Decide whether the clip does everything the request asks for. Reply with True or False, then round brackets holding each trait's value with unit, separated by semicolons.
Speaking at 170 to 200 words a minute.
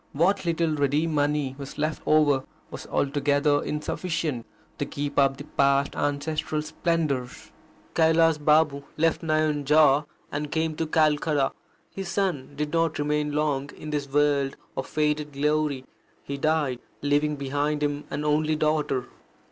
False (140 wpm)